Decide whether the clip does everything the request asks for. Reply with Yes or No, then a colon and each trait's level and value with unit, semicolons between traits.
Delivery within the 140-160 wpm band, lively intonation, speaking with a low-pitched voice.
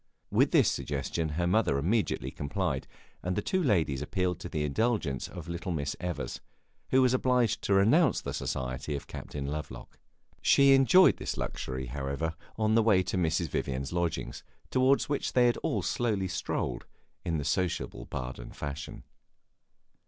Yes: average, 155 wpm; wide, 7.8 semitones; very low, 85 Hz